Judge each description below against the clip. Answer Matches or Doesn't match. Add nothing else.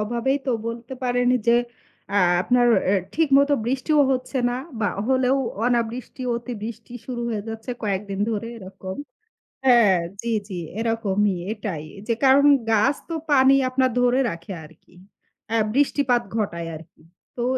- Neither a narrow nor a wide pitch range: Matches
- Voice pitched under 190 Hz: Doesn't match